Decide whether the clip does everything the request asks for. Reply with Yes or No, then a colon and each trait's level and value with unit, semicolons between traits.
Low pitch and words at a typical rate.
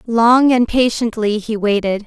No: high, 225 Hz; average, 145 wpm